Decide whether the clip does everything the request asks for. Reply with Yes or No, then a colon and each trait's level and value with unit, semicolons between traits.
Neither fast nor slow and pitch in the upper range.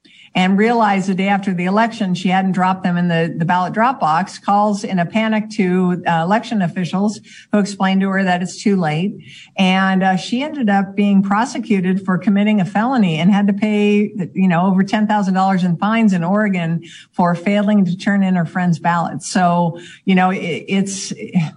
Yes: average, 190 wpm; high, 195 Hz